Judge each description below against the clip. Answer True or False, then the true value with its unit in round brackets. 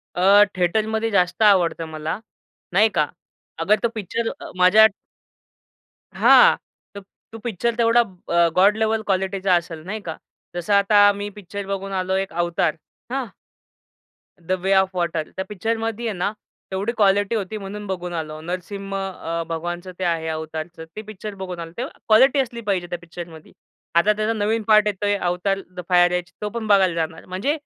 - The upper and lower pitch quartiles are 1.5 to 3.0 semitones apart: False (3.4 semitones)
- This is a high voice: True (195 Hz)